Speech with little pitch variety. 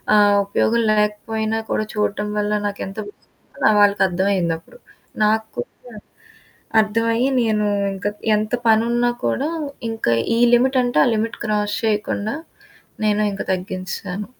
Yes: narrow, 1.7 semitones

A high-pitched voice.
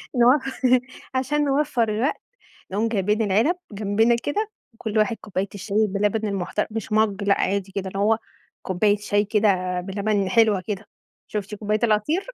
Yes: high, 210 Hz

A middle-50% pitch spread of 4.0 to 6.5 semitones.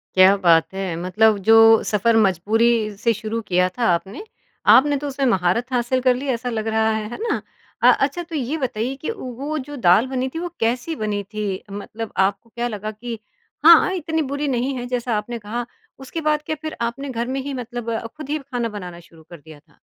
Yes: average, 4.4 semitones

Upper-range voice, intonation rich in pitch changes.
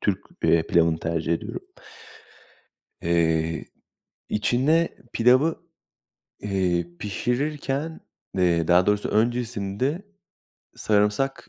No: low, 105 Hz; wide, 7.2 semitones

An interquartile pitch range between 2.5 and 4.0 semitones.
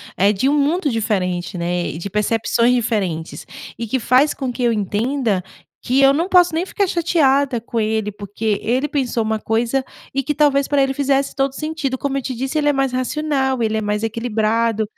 No: average, 4.4 semitones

